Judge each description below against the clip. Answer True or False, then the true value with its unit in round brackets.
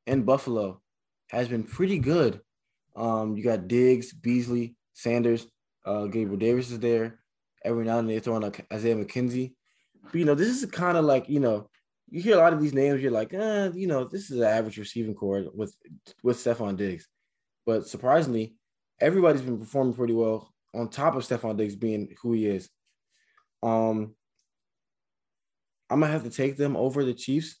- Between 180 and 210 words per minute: True (185 wpm)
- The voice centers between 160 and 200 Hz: False (120 Hz)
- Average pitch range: True (3.5 semitones)